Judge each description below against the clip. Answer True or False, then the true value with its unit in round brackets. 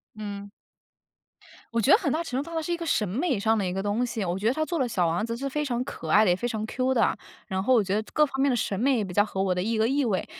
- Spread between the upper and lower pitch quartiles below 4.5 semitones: False (5.1 semitones)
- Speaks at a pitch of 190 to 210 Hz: False (225 Hz)